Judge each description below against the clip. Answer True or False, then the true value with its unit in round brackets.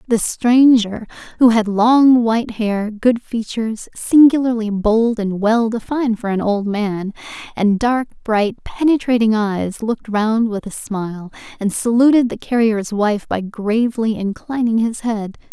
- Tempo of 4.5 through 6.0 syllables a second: False (4.2 syllables/s)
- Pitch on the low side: False (225 Hz)